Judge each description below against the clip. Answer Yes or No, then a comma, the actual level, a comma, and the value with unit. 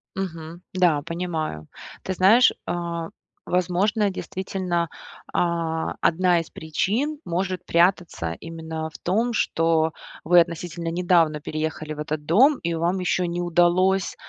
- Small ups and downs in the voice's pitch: Yes, narrow, 2.3 semitones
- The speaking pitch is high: No, medium, 170 Hz